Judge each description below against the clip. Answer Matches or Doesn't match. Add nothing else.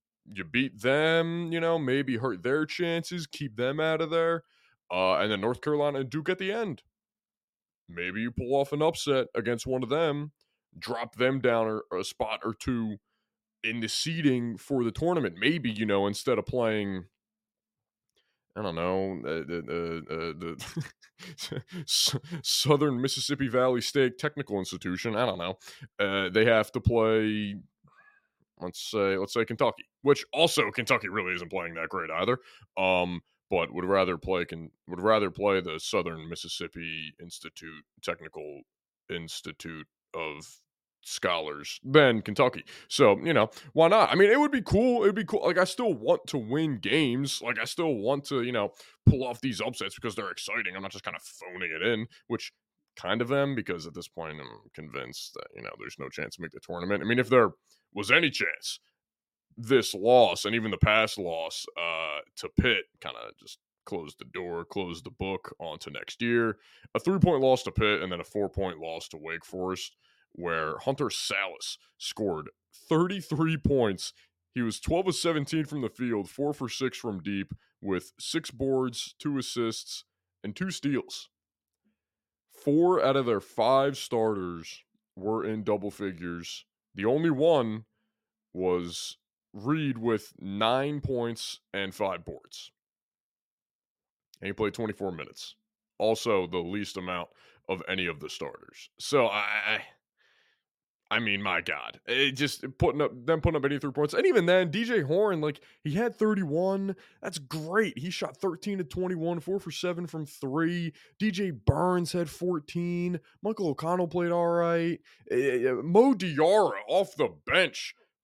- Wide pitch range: Matches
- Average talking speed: Matches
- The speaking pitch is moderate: Doesn't match